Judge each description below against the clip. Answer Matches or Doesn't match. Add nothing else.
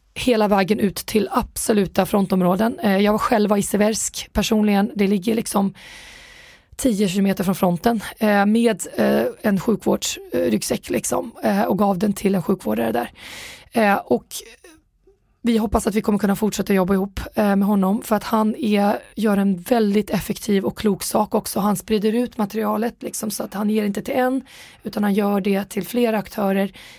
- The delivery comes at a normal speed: Matches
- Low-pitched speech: Doesn't match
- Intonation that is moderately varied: Doesn't match